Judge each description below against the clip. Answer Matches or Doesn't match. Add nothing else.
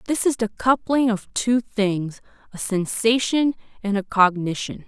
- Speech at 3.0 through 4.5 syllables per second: Matches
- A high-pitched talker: Matches